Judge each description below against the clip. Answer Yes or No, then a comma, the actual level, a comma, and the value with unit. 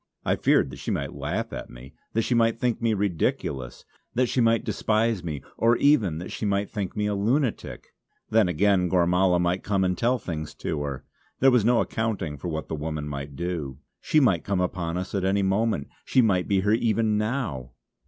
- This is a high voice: No, very low, 95 Hz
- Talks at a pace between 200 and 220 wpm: Yes, fast, 205 wpm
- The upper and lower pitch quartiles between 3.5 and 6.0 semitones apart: Yes, wide, 5.5 semitones